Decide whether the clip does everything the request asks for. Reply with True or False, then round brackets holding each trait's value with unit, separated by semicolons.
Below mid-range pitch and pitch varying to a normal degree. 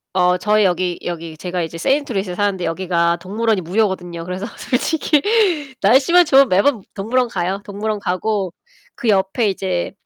False (195 Hz; 3.6 semitones)